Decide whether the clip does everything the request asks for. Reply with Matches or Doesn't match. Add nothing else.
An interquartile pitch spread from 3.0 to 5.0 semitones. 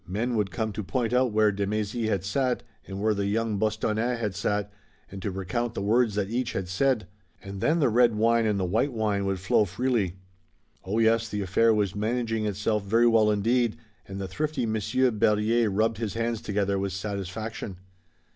Doesn't match